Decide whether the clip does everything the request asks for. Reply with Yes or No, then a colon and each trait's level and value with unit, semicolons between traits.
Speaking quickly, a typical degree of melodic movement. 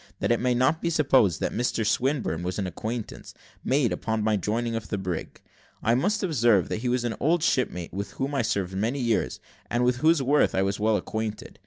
Yes: fast, 220 wpm; average, 4.3 semitones